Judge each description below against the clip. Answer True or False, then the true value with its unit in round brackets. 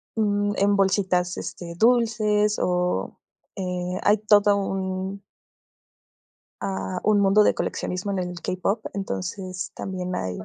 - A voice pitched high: True (195 Hz)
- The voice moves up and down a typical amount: False (2.3 semitones)